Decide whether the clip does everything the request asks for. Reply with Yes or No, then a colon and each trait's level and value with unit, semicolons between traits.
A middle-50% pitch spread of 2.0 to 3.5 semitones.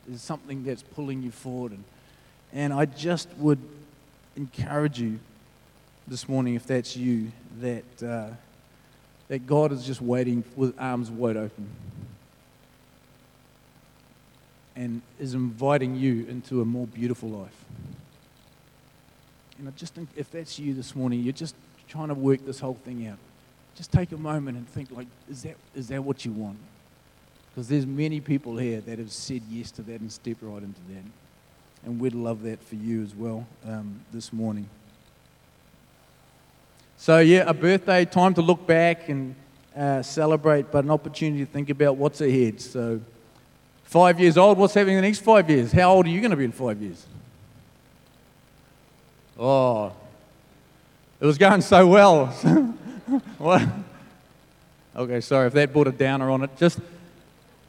No: average, 4.2 semitones